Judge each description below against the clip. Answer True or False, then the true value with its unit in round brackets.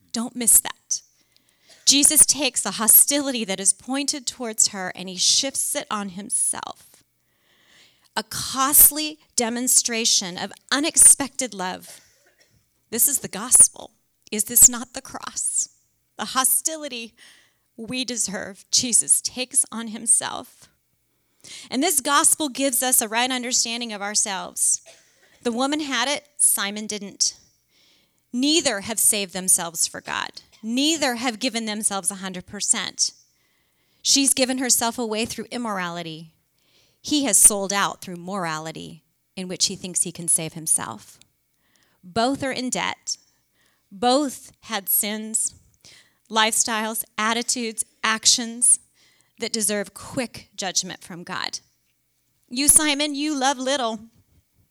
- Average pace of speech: False (120 wpm)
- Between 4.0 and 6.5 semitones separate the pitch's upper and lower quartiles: True (4.6 semitones)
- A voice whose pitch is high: True (230 Hz)